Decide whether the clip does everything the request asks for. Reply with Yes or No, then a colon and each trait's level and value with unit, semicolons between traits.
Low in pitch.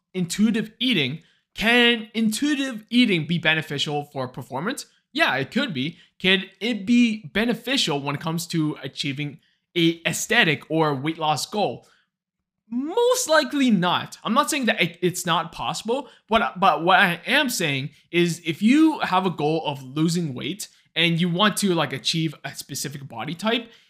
No: medium, 175 Hz